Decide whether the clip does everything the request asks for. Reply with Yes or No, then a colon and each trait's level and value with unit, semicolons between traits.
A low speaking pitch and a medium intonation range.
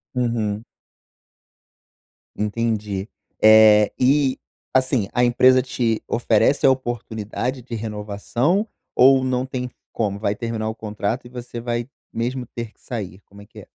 Yes: low, 115 Hz; average, 3.0 semitones